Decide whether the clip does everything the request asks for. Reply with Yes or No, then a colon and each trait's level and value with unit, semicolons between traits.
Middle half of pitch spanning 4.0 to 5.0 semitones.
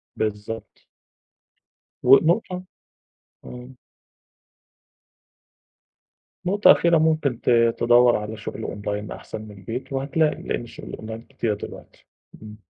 Yes: average, 4.5 semitones